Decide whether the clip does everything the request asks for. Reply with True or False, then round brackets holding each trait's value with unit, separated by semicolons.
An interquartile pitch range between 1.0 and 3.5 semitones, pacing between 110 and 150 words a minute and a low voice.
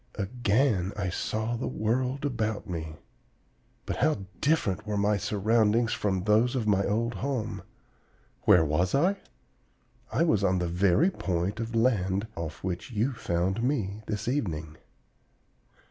False (4.2 semitones; 140 wpm; 105 Hz)